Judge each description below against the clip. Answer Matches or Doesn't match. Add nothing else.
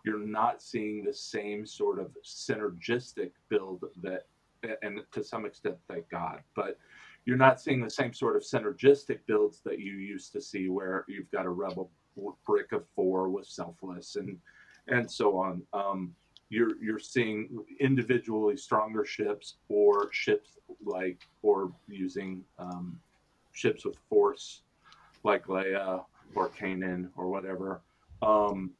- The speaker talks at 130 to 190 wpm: Matches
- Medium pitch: Doesn't match